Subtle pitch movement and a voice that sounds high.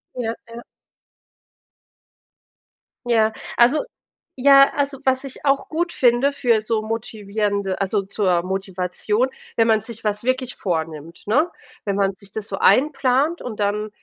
No: average, 4.4 semitones; high, 225 Hz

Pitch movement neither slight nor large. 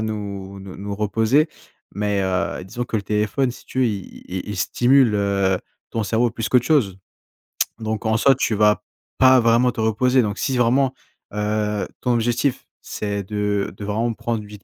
Yes: average, 3.0 semitones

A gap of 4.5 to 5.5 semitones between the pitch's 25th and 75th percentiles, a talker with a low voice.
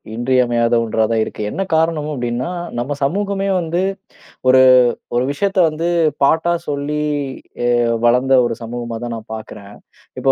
Yes: average, 5.2 semitones; low, 130 Hz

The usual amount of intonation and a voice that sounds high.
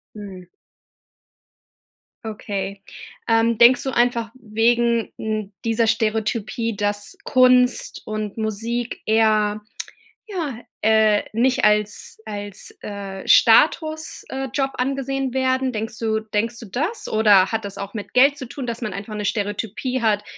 Yes: average, 3.1 semitones; high, 225 Hz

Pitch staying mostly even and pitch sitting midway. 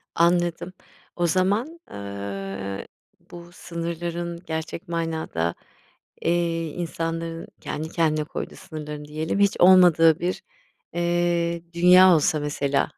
Yes: narrow, 2.1 semitones; medium, 165 Hz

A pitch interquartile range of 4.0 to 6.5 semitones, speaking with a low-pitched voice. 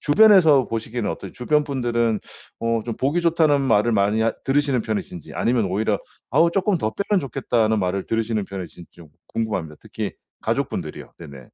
Yes: wide, 5.6 semitones; low, 115 Hz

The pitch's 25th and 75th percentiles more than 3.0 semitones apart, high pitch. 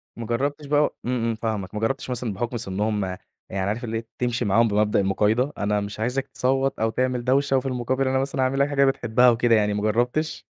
No: average, 3.6 semitones; low, 120 Hz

